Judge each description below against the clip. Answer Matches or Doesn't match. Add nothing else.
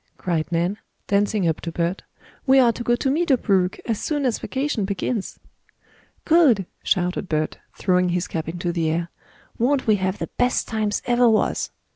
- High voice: Matches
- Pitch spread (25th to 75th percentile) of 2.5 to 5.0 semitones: Doesn't match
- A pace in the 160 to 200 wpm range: Matches